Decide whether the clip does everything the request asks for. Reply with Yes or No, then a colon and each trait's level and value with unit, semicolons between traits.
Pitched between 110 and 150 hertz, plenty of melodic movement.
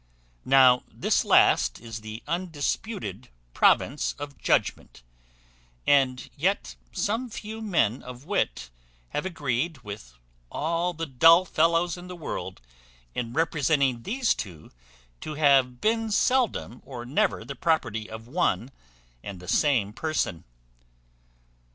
Yes: medium, 140 Hz; wide, 6.5 semitones